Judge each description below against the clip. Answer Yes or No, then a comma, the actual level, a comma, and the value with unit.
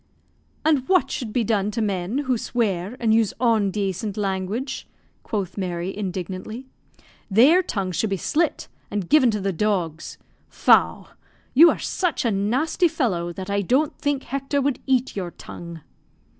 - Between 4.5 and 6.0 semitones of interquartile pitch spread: Yes, wide, 5.5 semitones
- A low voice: No, high, 215 Hz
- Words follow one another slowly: No, average, 155 wpm